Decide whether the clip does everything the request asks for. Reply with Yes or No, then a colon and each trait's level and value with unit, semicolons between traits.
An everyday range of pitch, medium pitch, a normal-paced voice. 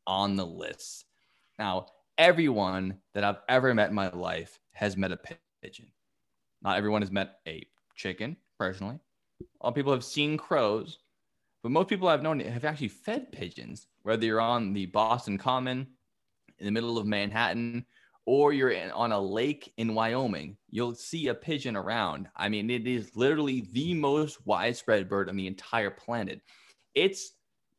No: average, 4.5 semitones; low, 115 Hz; average, 160 wpm